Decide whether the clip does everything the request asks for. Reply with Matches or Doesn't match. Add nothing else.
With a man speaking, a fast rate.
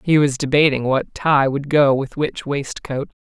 Doesn't match